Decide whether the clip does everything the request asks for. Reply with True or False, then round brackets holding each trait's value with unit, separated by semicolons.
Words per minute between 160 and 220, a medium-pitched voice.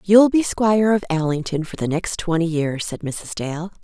True (205 wpm; 175 Hz)